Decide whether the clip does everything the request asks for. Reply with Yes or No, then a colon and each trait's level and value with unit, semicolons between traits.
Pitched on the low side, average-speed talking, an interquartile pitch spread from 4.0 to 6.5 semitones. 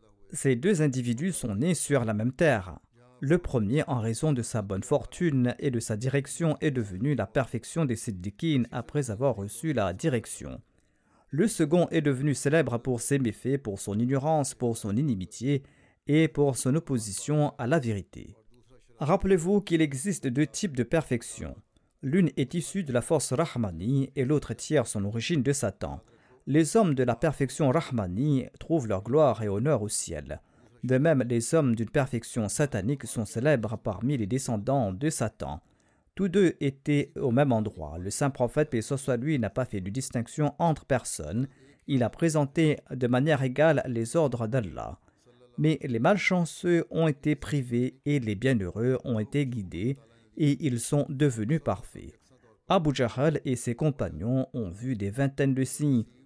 Yes: low, 130 Hz; average, 165 wpm; average, 4.7 semitones